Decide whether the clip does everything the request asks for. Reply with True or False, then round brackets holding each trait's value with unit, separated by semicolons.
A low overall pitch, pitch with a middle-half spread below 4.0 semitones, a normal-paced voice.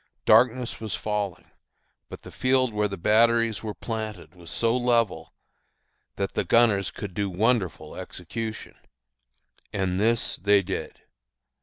False (105 Hz; 3.4 semitones; 130 wpm)